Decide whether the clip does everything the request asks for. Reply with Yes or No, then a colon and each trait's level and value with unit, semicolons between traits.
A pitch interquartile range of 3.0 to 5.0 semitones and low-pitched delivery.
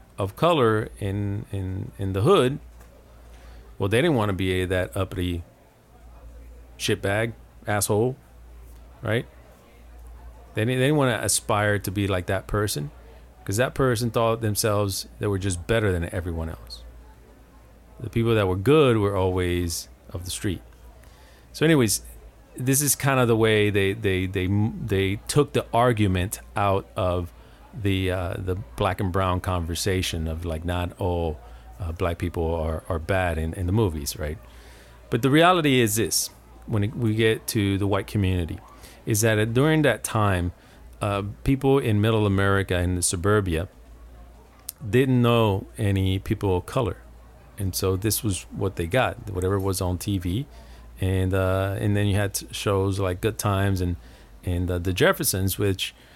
Yes: average, 4.2 semitones; very low, 95 Hz